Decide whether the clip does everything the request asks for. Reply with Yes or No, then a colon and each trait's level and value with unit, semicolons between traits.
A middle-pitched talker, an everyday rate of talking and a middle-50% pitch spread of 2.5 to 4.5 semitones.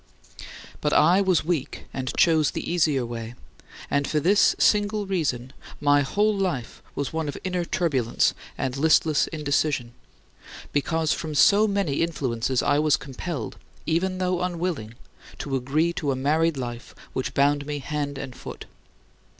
Yes: medium, 150 Hz; average, 150 wpm; average, 4.2 semitones